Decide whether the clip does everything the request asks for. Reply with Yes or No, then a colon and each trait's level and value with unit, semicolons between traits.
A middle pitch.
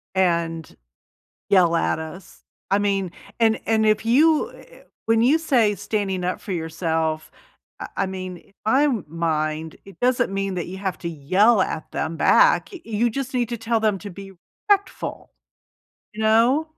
No: high, 195 Hz